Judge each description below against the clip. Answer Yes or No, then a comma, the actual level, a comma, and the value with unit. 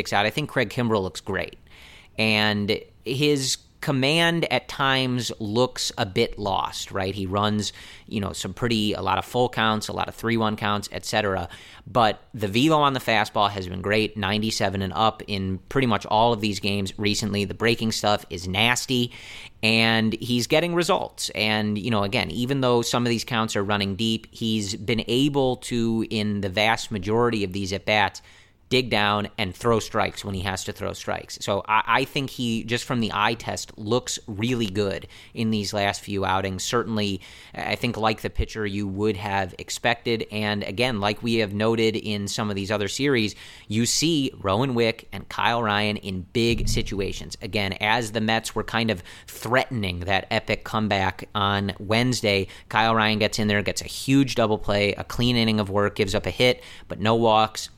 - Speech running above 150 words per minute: Yes, average, 195 wpm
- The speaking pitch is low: Yes, low, 110 Hz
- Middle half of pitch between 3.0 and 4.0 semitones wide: No, narrow, 2.6 semitones